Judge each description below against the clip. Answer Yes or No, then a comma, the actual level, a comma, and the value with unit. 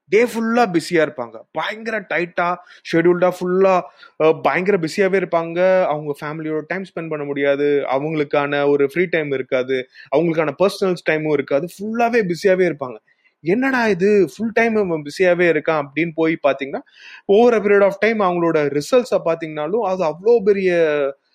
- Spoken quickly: Yes, fast, 135 wpm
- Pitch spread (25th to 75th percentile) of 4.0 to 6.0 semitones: Yes, average, 4.7 semitones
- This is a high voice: No, medium, 175 Hz